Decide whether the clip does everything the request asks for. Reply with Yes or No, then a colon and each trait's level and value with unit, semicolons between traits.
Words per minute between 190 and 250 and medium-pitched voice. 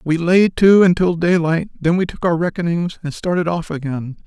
Yes: average, 195 wpm; medium, 170 Hz